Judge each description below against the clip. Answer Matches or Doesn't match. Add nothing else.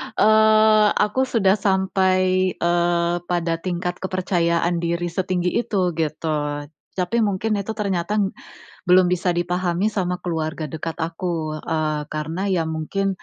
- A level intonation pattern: Matches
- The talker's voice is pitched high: Doesn't match